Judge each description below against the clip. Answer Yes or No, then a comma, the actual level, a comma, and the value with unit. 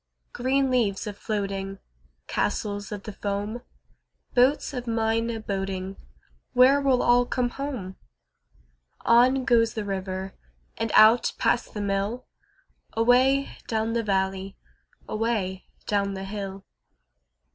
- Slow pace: Yes, slow, 120 wpm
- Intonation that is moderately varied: Yes, average, 3.7 semitones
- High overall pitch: Yes, high, 220 Hz